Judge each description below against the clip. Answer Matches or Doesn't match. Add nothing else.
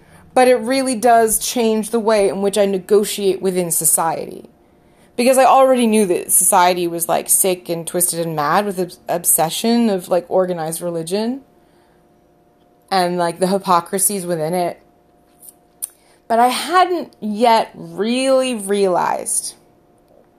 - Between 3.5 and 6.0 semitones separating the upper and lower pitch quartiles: Matches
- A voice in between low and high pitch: Doesn't match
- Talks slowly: Matches